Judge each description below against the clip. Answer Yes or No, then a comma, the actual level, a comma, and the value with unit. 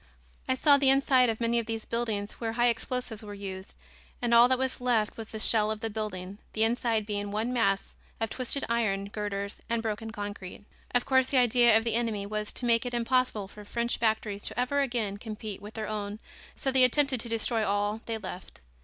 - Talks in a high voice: Yes, high, 225 Hz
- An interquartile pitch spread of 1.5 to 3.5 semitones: Yes, narrow, 2.6 semitones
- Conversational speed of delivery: No, fast, 215 wpm